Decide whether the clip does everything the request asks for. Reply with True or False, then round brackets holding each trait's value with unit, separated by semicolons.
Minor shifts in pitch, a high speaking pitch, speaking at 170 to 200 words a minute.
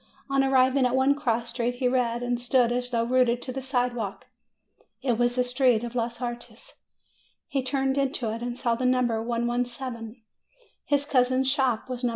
True (1.6 semitones; 245 Hz; 185 wpm)